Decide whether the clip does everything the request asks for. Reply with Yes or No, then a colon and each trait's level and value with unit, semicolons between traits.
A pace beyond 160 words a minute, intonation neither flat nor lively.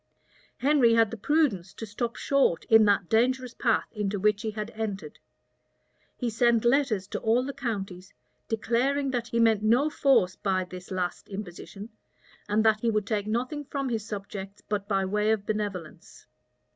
Yes: average, 170 wpm; average, 3.0 semitones